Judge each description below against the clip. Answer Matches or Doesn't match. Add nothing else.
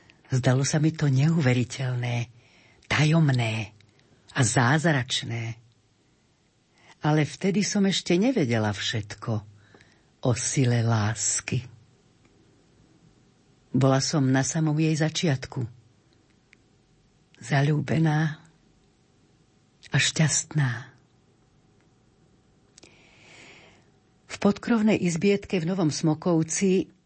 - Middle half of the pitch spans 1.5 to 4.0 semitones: Doesn't match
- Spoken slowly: Matches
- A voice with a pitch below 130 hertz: Doesn't match